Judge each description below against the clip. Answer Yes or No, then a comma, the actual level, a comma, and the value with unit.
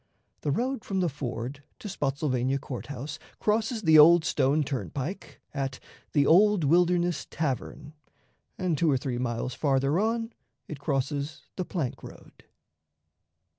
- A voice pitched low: No, medium, 150 Hz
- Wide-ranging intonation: No, average, 4.8 semitones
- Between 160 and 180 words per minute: No, slow, 135 wpm